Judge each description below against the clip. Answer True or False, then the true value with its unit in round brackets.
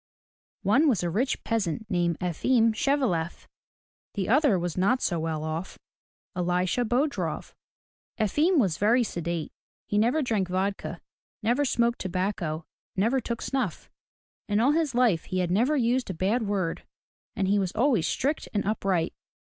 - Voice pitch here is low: False (205 Hz)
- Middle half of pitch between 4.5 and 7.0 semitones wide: True (5.6 semitones)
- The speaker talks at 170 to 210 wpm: False (160 wpm)